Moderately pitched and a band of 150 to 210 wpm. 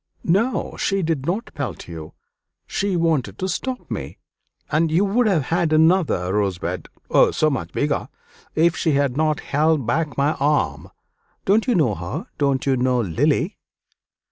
Yes: medium, 150 Hz; average, 160 wpm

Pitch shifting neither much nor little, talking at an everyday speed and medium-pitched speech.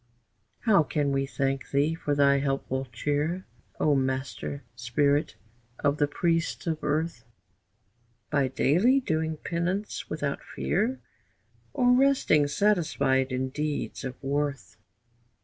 No: average, 3.5 semitones; slow, 115 wpm; medium, 145 Hz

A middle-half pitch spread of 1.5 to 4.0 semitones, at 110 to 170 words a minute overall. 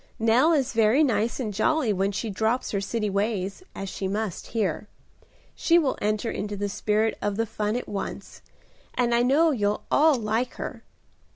No: average, 3.3 semitones; average, 180 wpm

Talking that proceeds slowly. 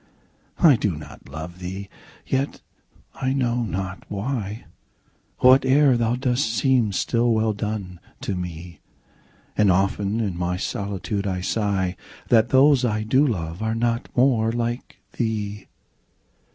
Yes: slow, 130 wpm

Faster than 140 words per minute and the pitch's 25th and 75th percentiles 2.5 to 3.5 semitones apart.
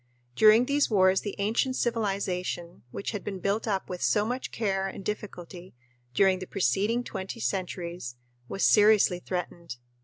Yes: average, 150 wpm; average, 2.9 semitones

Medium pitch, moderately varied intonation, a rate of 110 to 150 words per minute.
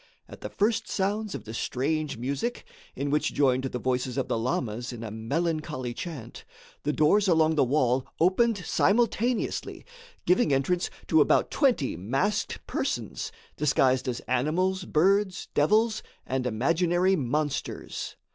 No: medium, 150 Hz; wide, 6.6 semitones; slow, 135 wpm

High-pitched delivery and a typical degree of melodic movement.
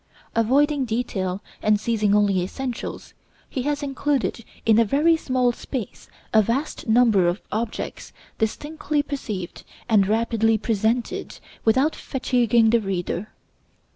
Yes: high, 230 Hz; average, 3.9 semitones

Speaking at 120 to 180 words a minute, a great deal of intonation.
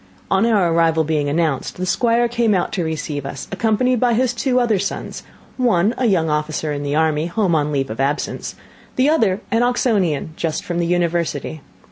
No: average, 190 wpm; wide, 6.7 semitones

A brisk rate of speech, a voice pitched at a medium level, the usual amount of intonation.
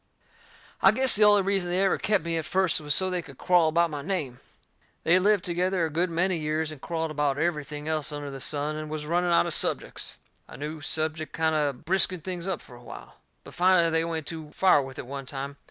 Yes: fast, 235 wpm; medium, 160 Hz; average, 3.3 semitones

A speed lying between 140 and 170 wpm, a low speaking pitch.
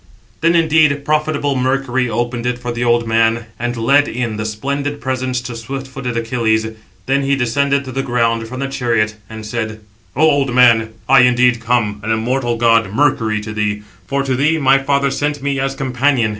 No: average, 190 wpm; low, 125 Hz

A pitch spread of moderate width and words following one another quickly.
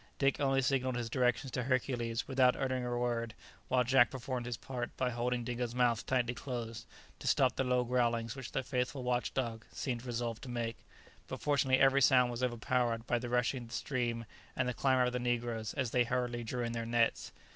No: narrow, 1.5 semitones; fast, 210 wpm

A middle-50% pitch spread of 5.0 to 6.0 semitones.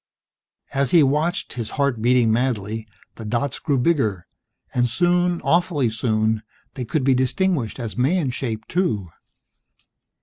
Yes: wide, 5.4 semitones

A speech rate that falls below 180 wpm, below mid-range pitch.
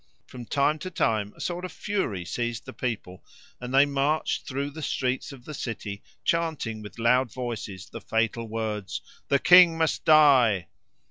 Yes: average, 165 wpm; low, 125 Hz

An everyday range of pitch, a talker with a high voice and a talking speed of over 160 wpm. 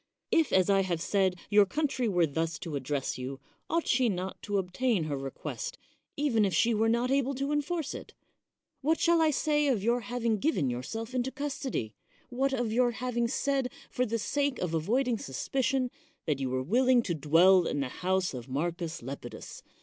No: wide, 7.9 semitones; high, 225 Hz; average, 190 wpm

